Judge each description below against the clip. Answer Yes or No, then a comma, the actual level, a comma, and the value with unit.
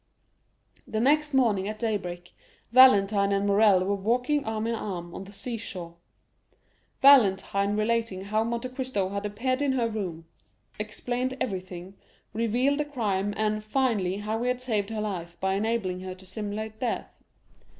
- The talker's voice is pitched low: No, high, 215 Hz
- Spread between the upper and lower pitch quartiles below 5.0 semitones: Yes, average, 3.5 semitones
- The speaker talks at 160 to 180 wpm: No, average, 150 wpm